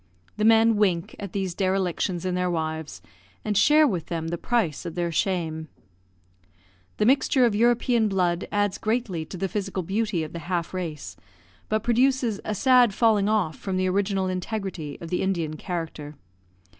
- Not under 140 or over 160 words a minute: No, average, 170 wpm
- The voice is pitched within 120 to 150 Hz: No, high, 190 Hz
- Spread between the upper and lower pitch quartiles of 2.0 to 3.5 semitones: No, average, 4.1 semitones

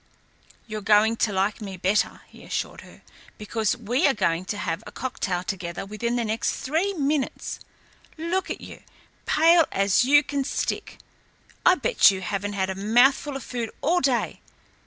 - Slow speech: No, average, 170 wpm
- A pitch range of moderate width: No, wide, 5.9 semitones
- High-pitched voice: Yes, high, 225 Hz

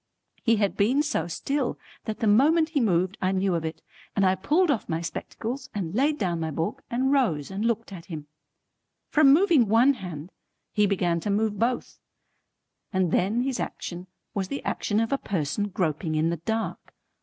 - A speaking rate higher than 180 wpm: Yes, average, 190 wpm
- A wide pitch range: Yes, wide, 6.4 semitones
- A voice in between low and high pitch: No, high, 205 Hz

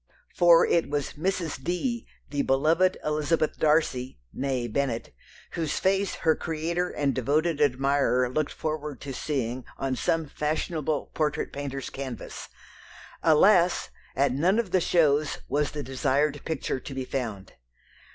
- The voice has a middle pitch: Yes, medium, 150 Hz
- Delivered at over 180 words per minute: No, slow, 135 wpm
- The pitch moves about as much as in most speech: Yes, average, 3.4 semitones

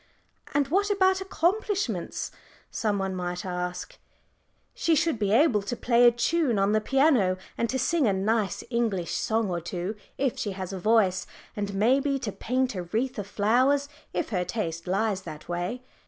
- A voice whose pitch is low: No, high, 220 Hz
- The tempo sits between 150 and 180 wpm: Yes, average, 175 wpm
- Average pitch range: No, wide, 5.9 semitones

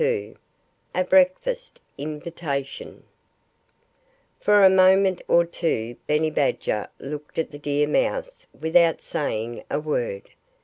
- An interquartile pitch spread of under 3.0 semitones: No, average, 4.5 semitones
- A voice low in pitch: No, medium, 160 Hz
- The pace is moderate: No, slow, 115 wpm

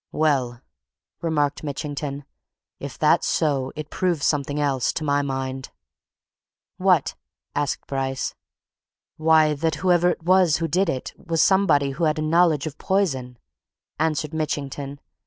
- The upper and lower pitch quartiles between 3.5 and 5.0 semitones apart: No, narrow, 2.6 semitones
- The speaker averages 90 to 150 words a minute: Yes, slow, 135 wpm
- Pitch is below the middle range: No, medium, 150 Hz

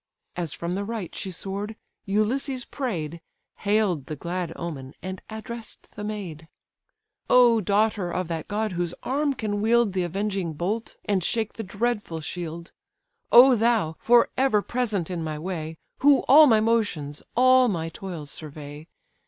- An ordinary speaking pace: Yes, average, 155 wpm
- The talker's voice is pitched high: Yes, high, 200 Hz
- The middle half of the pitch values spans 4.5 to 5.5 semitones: Yes, average, 5.2 semitones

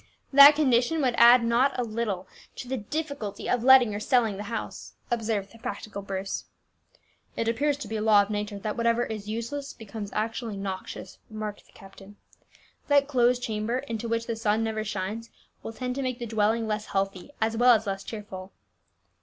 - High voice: Yes, high, 225 Hz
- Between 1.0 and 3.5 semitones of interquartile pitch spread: Yes, average, 2.7 semitones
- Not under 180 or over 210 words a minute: Yes, average, 185 wpm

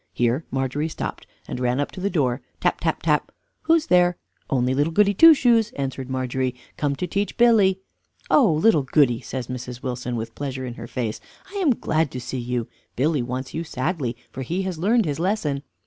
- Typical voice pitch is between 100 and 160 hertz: Yes, medium, 140 Hz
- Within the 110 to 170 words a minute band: No, average, 195 wpm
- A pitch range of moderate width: No, wide, 6.5 semitones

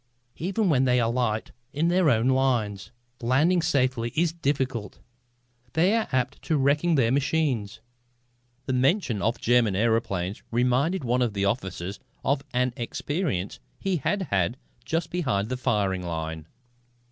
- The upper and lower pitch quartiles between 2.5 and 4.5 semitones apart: No, wide, 5.5 semitones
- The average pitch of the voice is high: No, low, 125 Hz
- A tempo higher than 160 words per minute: No, average, 140 wpm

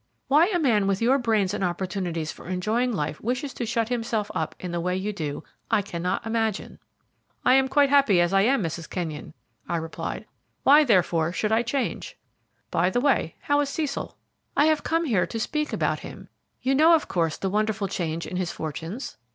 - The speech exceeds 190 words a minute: Yes, average, 200 wpm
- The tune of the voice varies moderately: No, wide, 7.0 semitones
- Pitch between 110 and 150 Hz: No, high, 210 Hz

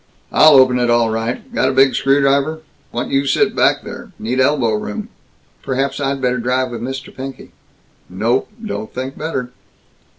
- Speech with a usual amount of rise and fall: No, narrow, 2.3 semitones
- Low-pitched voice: Yes, low, 130 Hz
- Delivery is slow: No, average, 165 wpm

